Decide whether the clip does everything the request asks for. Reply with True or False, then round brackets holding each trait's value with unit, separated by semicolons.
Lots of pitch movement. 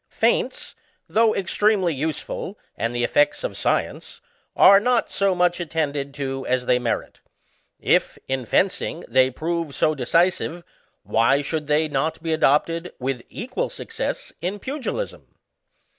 True (5.8 semitones)